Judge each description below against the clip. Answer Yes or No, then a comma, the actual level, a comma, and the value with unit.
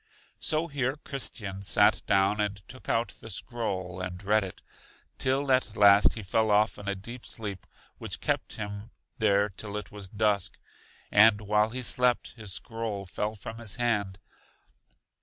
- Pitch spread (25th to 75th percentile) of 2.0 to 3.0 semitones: Yes, average, 2.7 semitones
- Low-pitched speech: Yes, low, 105 Hz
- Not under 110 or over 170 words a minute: Yes, average, 160 wpm